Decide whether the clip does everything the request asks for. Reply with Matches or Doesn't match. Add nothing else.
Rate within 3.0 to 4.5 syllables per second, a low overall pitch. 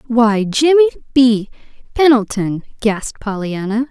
Doesn't match